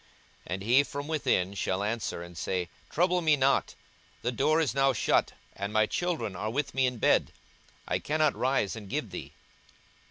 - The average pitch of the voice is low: Yes, low, 125 Hz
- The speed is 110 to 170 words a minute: No, average, 185 wpm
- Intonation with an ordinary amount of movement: No, wide, 6.7 semitones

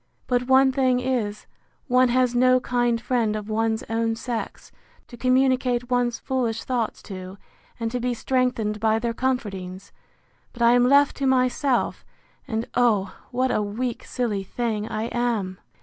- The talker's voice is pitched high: Yes, high, 240 Hz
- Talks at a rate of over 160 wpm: No, average, 155 wpm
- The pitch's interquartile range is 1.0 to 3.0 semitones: Yes, narrow, 2.4 semitones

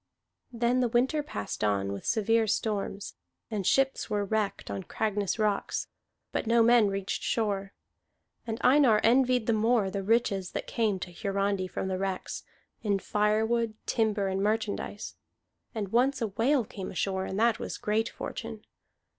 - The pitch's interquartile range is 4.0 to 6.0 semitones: No, average, 2.9 semitones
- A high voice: Yes, high, 215 Hz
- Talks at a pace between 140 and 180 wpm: Yes, average, 155 wpm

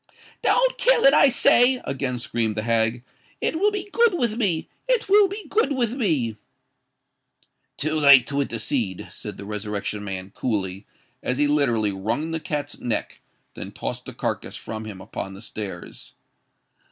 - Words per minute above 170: No, average, 165 wpm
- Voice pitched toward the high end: No, low, 135 Hz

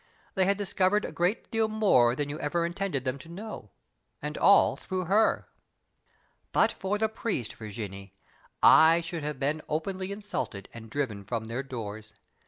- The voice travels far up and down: Yes, wide, 8.4 semitones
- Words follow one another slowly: No, average, 165 wpm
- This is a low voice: No, medium, 160 Hz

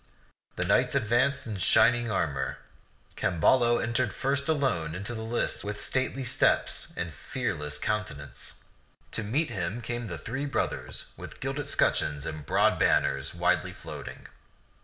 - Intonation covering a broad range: Yes, wide, 6.3 semitones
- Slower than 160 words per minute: Yes, slow, 135 wpm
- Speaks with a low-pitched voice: Yes, low, 110 Hz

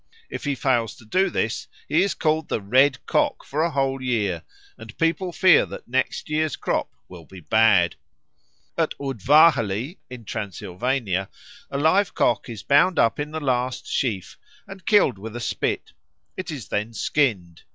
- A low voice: Yes, low, 130 Hz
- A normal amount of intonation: No, wide, 6.0 semitones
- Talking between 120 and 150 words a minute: No, average, 165 wpm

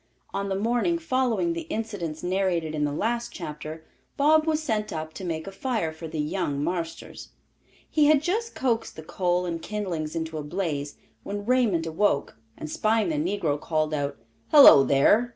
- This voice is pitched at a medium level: Yes, medium, 180 Hz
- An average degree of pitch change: No, wide, 6.2 semitones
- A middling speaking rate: Yes, average, 175 wpm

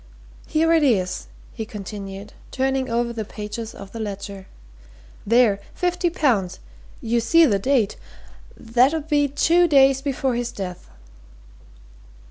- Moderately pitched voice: No, high, 235 Hz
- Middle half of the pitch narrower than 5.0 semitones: No, wide, 5.4 semitones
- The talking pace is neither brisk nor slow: No, slow, 130 wpm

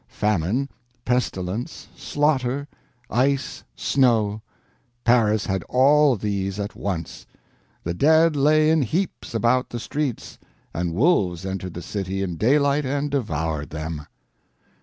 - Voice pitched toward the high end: No, low, 115 Hz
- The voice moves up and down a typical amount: No, wide, 6.8 semitones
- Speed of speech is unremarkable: No, slow, 115 wpm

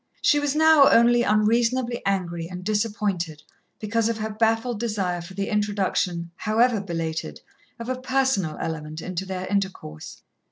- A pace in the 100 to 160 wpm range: Yes, average, 145 wpm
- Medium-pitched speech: No, high, 210 Hz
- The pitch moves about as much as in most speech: Yes, average, 4.7 semitones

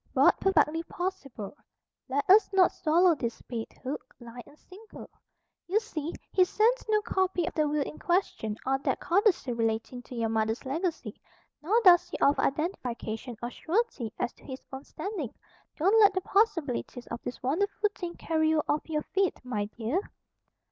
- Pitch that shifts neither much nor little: No, wide, 7.4 semitones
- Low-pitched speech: No, very high, 310 Hz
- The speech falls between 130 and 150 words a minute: No, average, 170 wpm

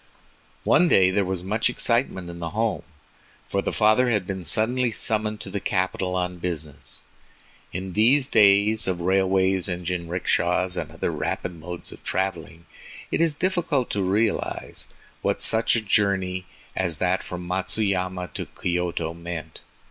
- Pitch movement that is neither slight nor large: Yes, average, 3.3 semitones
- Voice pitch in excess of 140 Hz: No, very low, 95 Hz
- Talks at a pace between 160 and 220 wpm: No, average, 150 wpm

